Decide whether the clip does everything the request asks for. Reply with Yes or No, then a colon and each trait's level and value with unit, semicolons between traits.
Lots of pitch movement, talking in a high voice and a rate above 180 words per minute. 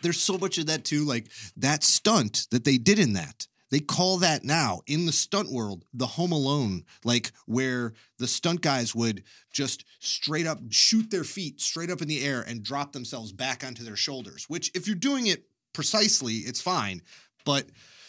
No: wide, 6.3 semitones; medium, 140 Hz; average, 190 wpm